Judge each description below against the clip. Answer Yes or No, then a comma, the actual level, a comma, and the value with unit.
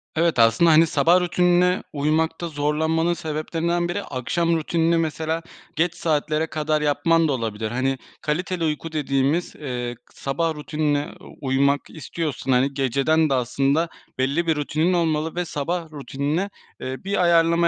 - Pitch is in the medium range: Yes, medium, 155 Hz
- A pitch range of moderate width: Yes, average, 3.1 semitones